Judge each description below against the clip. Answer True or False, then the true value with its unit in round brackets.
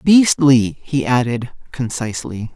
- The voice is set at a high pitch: False (130 Hz)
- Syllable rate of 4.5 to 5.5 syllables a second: False (4.1 syllables/s)